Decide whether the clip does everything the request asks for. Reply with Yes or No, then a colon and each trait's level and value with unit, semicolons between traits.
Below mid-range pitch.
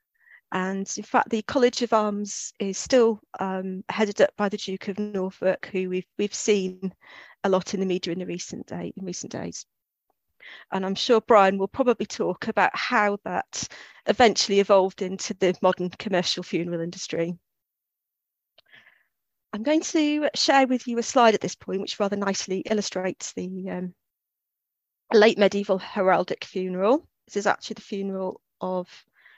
No: high, 195 Hz